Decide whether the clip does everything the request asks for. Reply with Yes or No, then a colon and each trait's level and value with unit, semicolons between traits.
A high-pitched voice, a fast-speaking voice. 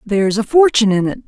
Yes: high, 225 Hz; fast, 235 wpm